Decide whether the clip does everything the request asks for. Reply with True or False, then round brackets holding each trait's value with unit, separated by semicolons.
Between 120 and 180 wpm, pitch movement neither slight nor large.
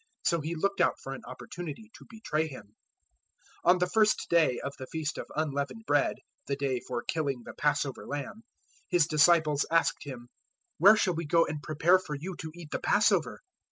False (195 wpm; 3.7 semitones)